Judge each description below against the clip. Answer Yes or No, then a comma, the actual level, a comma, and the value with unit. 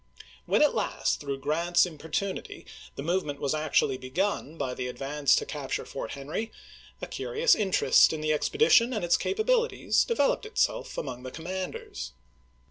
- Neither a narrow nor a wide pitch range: No, wide, 6.7 semitones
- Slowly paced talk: No, average, 155 wpm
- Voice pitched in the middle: Yes, medium, 160 Hz